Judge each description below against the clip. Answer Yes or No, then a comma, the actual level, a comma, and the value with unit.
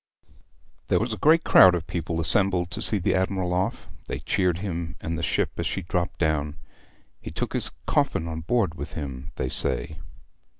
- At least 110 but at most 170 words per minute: No, average, 185 wpm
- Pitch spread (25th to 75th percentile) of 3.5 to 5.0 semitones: No, average, 3.0 semitones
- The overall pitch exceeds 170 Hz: No, very low, 85 Hz